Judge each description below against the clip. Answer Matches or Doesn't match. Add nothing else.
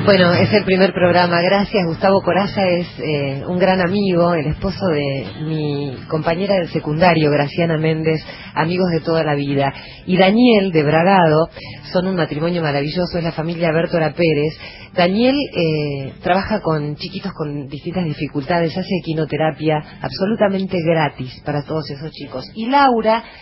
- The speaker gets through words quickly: Doesn't match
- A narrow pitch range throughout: Doesn't match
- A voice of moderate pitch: Matches